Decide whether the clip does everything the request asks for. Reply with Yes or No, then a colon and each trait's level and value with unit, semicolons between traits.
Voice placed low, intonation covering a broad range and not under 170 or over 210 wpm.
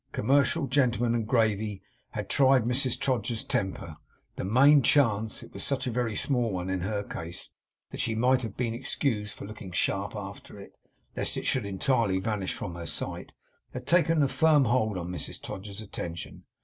No: low, 110 Hz; average, 4.6 semitones; average, 180 wpm